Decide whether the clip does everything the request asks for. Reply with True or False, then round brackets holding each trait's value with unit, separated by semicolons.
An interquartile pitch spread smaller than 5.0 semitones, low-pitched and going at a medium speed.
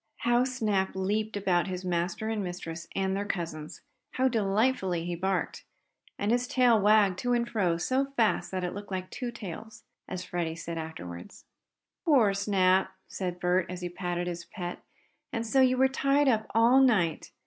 False (4.5 semitones; 195 Hz; 175 wpm)